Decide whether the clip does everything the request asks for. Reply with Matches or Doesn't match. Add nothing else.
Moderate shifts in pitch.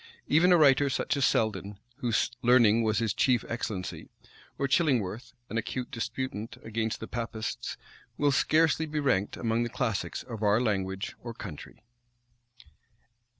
Matches